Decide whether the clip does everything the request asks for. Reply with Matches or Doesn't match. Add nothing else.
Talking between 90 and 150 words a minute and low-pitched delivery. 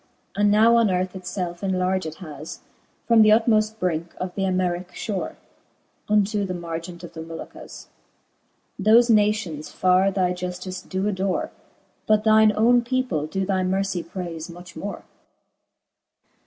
Doesn't match